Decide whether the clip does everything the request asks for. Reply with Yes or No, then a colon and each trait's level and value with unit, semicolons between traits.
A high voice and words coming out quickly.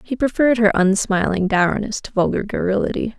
No: high, 210 Hz; average, 150 wpm